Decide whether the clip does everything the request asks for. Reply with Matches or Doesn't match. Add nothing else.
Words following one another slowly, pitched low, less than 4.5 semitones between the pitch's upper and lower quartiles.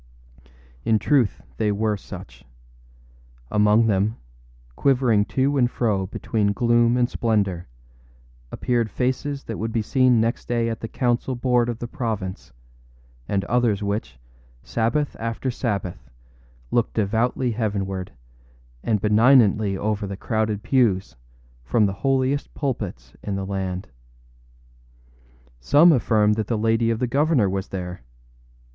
Matches